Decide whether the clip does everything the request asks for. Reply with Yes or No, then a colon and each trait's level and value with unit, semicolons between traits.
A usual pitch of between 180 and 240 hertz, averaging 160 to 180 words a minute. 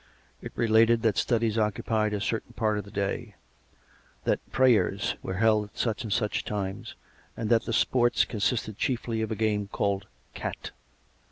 No: low, 110 Hz; average, 170 wpm